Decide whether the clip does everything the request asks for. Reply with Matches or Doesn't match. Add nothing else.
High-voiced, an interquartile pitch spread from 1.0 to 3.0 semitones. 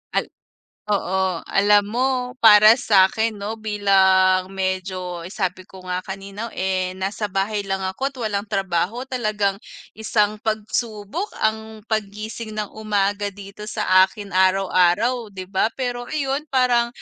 Matches